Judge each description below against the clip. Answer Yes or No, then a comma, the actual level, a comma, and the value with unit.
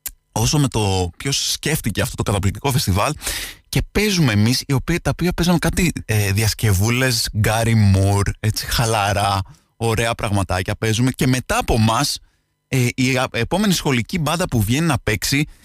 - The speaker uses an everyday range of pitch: Yes, average, 5.0 semitones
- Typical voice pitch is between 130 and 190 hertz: No, low, 115 Hz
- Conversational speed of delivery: Yes, average, 140 wpm